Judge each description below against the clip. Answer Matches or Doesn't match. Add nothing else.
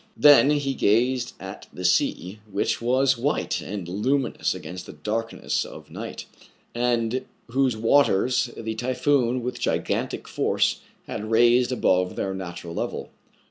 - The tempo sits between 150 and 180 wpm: Doesn't match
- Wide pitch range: Doesn't match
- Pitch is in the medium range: Doesn't match